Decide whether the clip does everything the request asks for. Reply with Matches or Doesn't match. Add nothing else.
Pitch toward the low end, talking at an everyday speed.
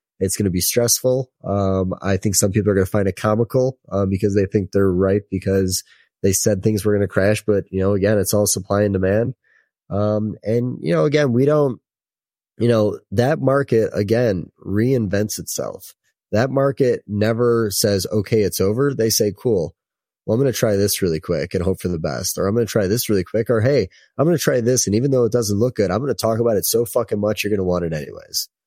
Doesn't match